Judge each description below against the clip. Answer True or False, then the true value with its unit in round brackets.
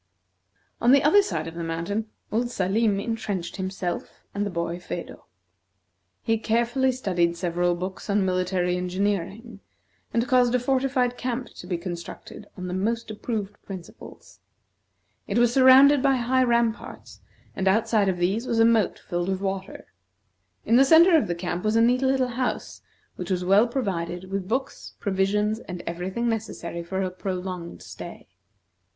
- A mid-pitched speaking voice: False (205 Hz)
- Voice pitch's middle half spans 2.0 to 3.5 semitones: False (4.8 semitones)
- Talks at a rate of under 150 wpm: False (160 wpm)